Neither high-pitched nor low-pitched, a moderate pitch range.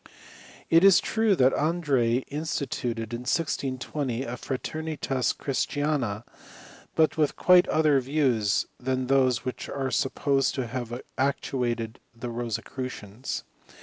No: low, 130 Hz; average, 3.5 semitones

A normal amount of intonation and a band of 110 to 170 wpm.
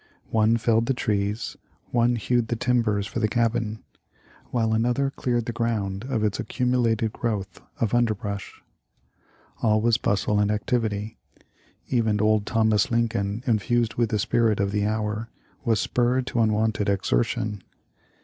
No: narrow, 2.0 semitones; average, 145 wpm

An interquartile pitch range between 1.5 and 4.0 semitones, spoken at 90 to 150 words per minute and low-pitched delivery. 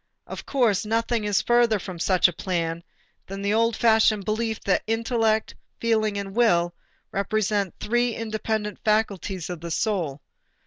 No: average, 2.9 semitones; average, 145 wpm; high, 215 Hz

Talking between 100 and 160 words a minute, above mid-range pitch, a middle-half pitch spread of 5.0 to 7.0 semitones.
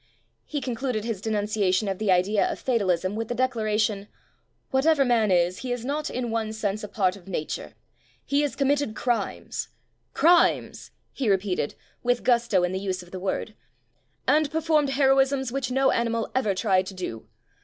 No: average, 180 wpm; high, 225 Hz; average, 5.3 semitones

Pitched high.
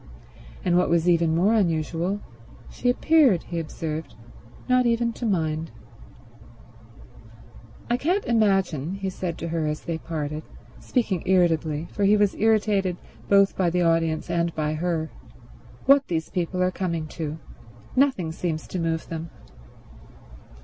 No: medium, 175 Hz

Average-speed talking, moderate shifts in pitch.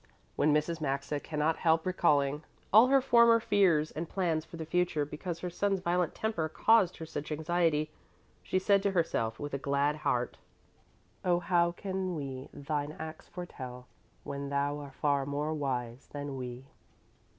Yes: average, 160 wpm; average, 3.9 semitones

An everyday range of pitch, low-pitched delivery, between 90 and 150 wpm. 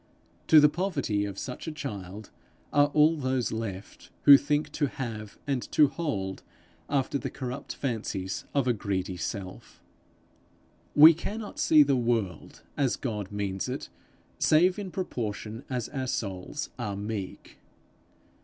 No: wide, 6.2 semitones; low, 125 Hz; average, 140 wpm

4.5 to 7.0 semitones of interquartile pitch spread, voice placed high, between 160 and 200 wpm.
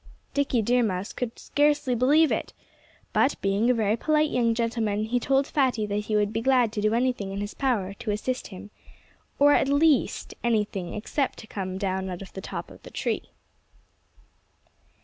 No: average, 4.1 semitones; high, 225 Hz; average, 185 wpm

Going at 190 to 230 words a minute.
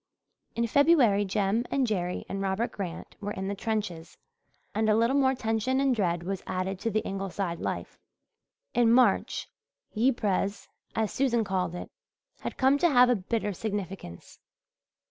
No: average, 155 wpm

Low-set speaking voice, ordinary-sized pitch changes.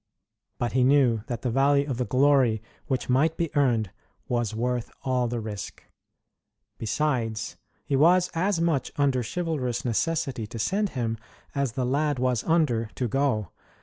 Yes: low, 130 Hz; average, 3.7 semitones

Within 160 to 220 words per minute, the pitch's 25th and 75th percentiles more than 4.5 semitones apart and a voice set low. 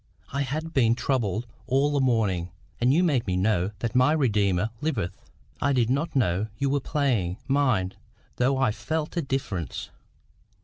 Yes: average, 165 wpm; average, 5.2 semitones; low, 125 Hz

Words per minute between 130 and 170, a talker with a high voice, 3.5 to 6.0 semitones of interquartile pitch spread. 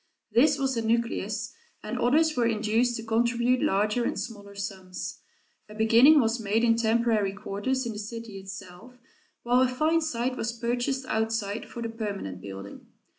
No: average, 165 wpm; high, 230 Hz; average, 2.7 semitones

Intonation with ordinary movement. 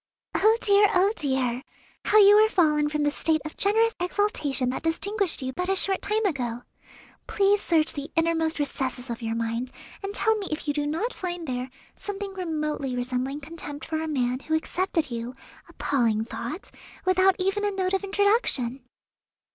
No: wide, 6.7 semitones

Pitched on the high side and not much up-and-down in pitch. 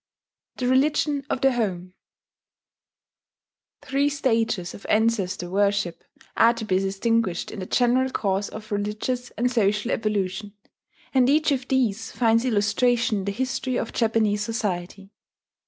No: high, 225 Hz; average, 3.9 semitones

